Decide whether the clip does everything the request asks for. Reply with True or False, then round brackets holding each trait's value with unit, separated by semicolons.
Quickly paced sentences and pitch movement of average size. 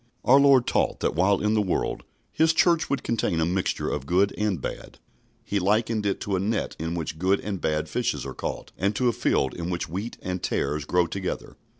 True (220 wpm; 3.9 semitones)